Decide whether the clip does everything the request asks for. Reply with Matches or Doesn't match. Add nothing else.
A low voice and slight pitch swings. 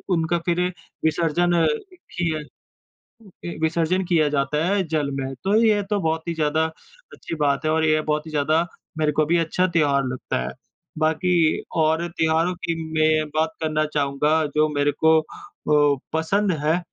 Doesn't match